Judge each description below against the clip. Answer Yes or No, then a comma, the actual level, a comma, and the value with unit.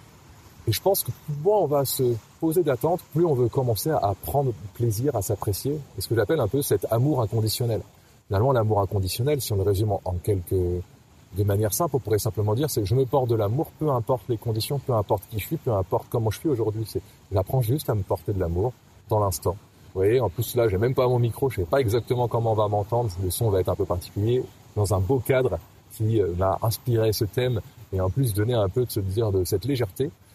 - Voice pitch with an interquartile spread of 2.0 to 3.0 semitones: No, average, 3.9 semitones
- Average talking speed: No, fast, 245 wpm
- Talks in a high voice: No, low, 115 Hz